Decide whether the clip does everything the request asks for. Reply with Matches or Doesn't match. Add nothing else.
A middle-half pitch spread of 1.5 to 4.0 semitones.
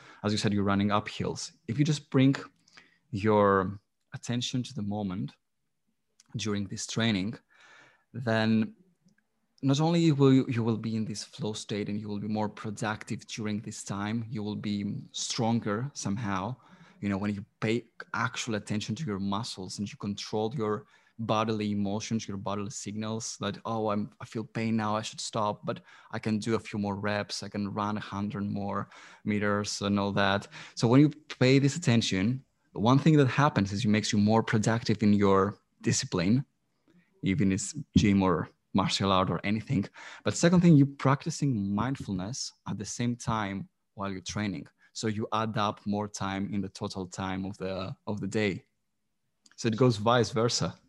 Matches